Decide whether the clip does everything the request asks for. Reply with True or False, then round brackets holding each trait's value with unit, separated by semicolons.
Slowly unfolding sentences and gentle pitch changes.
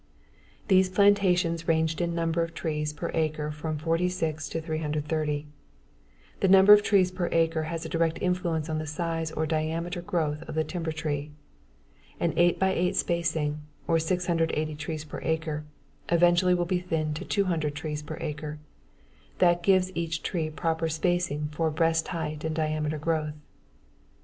False (160 wpm; 2.0 semitones)